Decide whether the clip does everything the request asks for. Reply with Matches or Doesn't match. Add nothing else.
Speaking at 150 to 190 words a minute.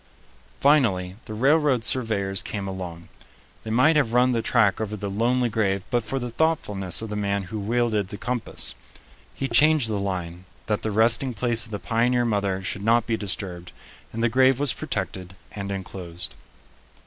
Matches